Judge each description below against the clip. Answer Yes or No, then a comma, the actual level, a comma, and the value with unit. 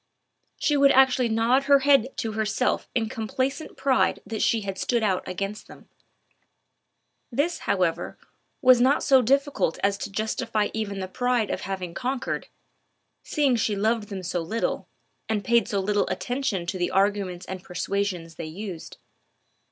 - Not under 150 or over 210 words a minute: Yes, average, 155 wpm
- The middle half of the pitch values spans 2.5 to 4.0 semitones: No, average, 4.7 semitones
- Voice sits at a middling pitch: No, high, 220 Hz